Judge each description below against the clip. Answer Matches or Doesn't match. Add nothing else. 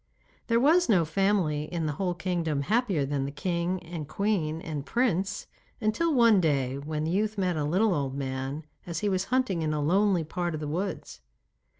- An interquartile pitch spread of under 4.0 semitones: Doesn't match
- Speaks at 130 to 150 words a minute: Doesn't match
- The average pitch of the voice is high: Doesn't match